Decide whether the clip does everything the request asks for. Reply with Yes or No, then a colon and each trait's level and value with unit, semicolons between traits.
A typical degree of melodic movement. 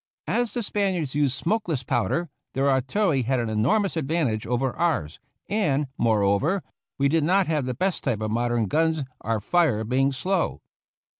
No: wide, 6.2 semitones